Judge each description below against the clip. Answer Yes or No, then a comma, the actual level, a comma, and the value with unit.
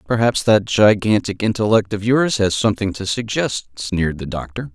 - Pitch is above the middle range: No, low, 105 Hz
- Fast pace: No, average, 165 wpm